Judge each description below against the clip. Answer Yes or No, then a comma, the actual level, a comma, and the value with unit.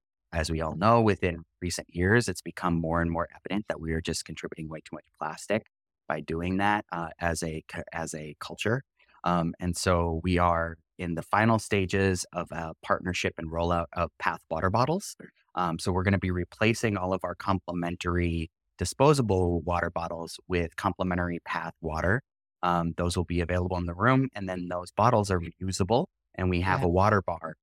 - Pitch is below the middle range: Yes, very low, 90 Hz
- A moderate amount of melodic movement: No, narrow, 2.1 semitones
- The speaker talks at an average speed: Yes, average, 190 wpm